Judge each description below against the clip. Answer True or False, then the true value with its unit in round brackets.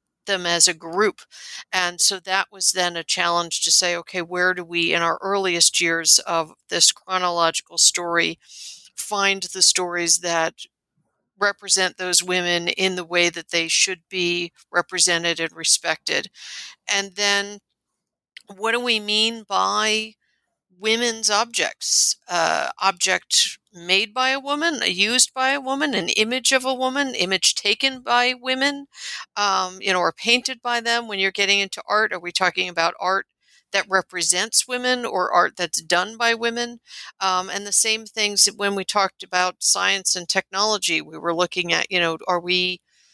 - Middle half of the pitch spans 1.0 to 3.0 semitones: False (3.8 semitones)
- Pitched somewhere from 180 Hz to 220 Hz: True (190 Hz)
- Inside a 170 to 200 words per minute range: False (160 wpm)